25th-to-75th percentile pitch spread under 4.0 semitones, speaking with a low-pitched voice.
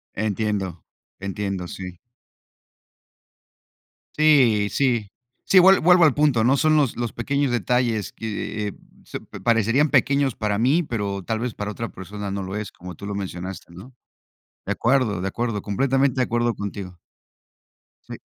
No: average, 4.8 semitones; low, 110 Hz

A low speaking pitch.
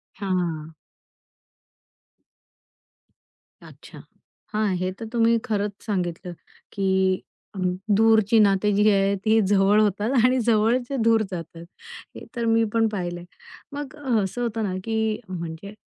No: high, 205 Hz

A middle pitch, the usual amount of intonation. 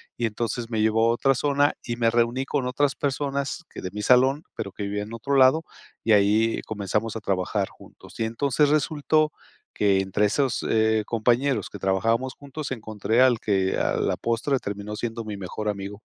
No: low, 115 Hz; average, 4.3 semitones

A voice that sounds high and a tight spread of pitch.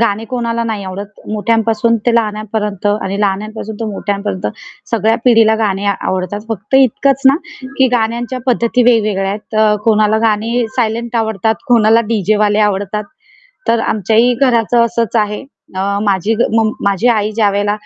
Yes: high, 220 Hz; narrow, 2.1 semitones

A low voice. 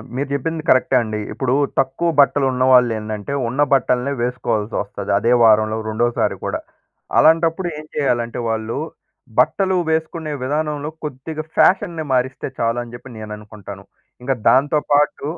Yes: low, 130 Hz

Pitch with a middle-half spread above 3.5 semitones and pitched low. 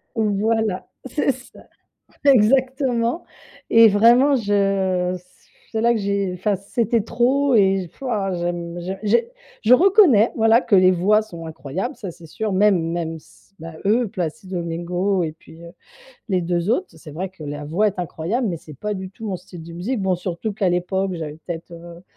No: average, 4.5 semitones; high, 195 Hz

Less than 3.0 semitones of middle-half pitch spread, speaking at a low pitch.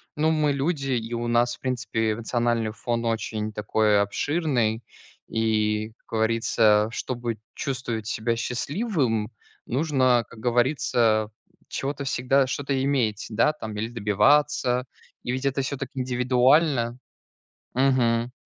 No: average, 3.3 semitones; low, 120 Hz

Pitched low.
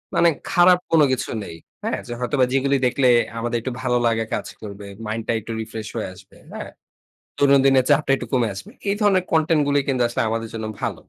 Yes: low, 130 Hz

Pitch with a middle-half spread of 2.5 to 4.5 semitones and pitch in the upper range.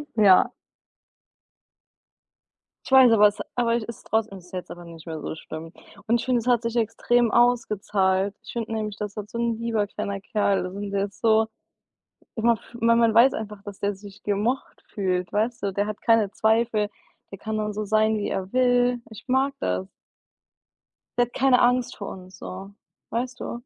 Yes: average, 2.9 semitones; high, 215 Hz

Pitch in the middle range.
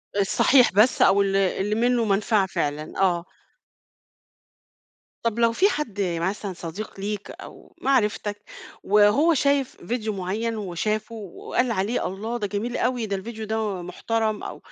No: high, 210 Hz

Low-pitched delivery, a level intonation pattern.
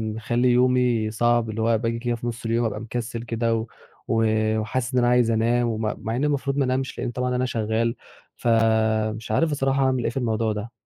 Yes: low, 120 Hz; narrow, 1.9 semitones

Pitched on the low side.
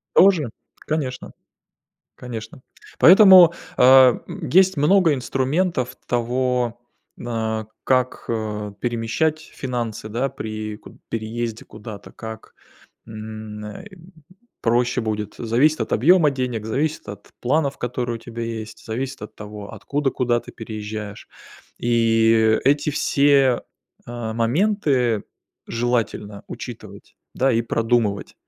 Yes: low, 120 Hz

